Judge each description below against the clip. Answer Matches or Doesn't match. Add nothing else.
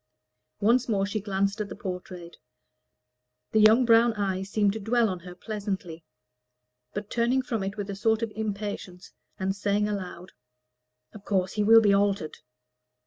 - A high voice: Matches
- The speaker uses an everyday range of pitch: Doesn't match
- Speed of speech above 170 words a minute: Doesn't match